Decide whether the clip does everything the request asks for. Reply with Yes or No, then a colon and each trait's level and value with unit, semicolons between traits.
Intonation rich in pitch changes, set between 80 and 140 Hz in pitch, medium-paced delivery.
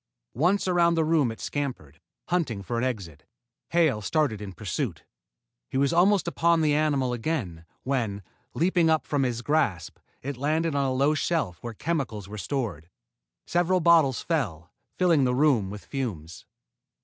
Yes: wide, 7.2 semitones; low, 135 Hz; average, 160 wpm